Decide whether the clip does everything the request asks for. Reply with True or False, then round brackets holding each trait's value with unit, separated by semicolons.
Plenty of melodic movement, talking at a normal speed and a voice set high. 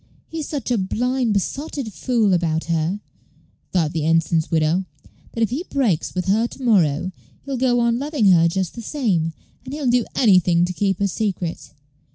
True (6.4 semitones; 180 wpm; 200 Hz)